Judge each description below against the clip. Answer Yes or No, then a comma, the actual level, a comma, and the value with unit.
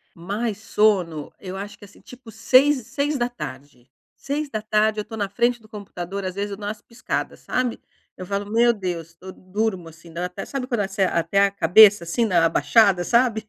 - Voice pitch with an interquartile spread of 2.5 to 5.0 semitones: Yes, average, 3.9 semitones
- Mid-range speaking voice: No, high, 205 Hz